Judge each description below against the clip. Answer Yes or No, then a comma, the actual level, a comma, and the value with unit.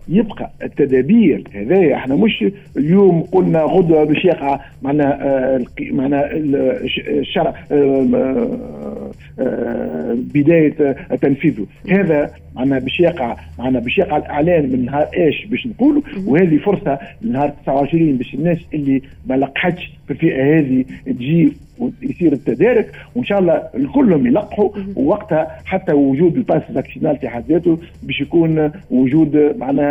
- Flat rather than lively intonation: No, average, 5.3 semitones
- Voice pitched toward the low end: No, medium, 155 Hz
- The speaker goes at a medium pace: Yes, average, 115 wpm